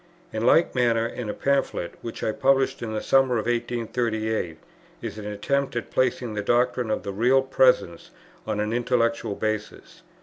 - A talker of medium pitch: No, low, 115 Hz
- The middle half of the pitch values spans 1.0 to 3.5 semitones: Yes, average, 2.7 semitones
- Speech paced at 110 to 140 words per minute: No, average, 170 wpm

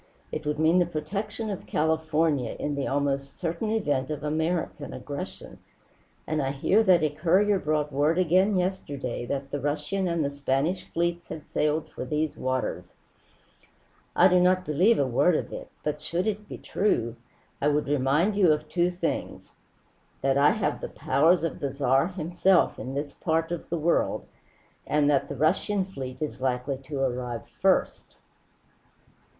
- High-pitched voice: No, medium, 155 Hz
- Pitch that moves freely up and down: No, average, 4.0 semitones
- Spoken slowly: No, average, 165 wpm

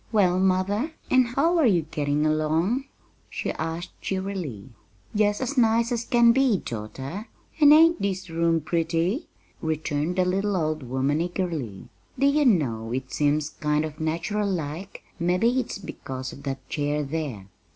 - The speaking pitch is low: No, medium, 170 Hz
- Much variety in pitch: Yes, wide, 6.0 semitones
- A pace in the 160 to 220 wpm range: No, average, 150 wpm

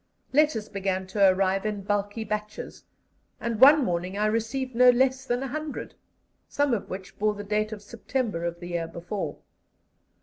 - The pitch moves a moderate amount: Yes, average, 4.3 semitones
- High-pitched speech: Yes, high, 210 Hz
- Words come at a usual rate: Yes, average, 165 wpm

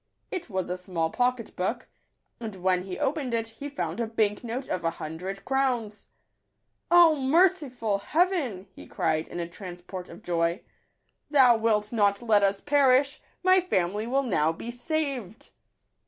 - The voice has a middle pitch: No, high, 225 Hz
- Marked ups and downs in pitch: Yes, wide, 6.5 semitones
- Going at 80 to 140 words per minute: No, average, 170 wpm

